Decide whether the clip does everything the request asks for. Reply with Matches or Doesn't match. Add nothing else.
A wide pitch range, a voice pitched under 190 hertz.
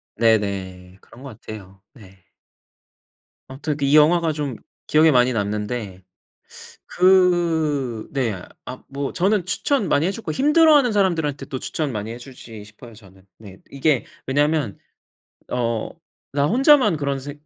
Matches